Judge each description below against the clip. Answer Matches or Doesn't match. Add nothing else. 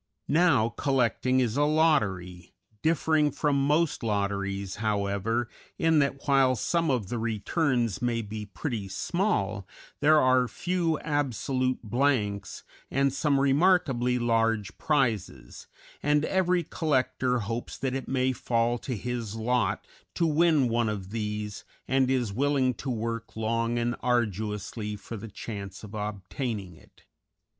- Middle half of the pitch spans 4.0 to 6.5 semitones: Matches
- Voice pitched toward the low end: Matches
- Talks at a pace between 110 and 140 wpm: Matches